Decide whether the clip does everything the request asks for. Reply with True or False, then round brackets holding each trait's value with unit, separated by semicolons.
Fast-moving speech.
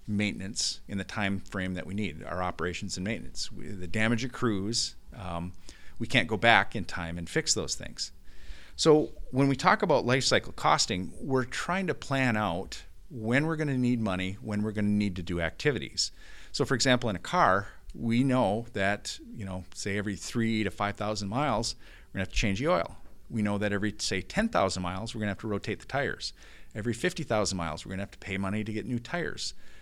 True (215 wpm)